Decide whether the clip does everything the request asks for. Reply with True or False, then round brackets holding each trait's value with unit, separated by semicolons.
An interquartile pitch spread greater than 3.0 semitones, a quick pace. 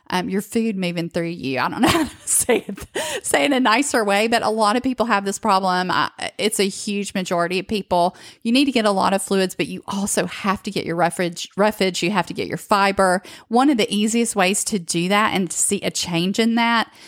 True (3.6 semitones; 255 wpm)